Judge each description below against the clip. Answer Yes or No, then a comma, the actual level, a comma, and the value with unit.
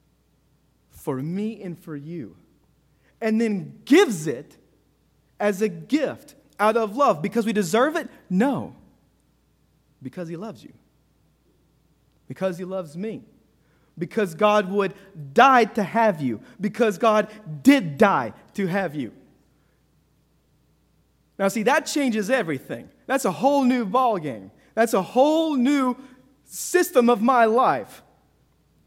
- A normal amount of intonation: No, wide, 6.0 semitones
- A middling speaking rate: No, slow, 125 wpm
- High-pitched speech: Yes, high, 215 Hz